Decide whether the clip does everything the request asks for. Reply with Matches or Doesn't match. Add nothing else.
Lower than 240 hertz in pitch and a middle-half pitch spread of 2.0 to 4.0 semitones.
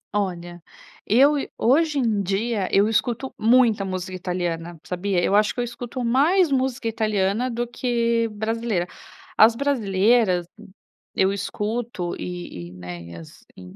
Doesn't match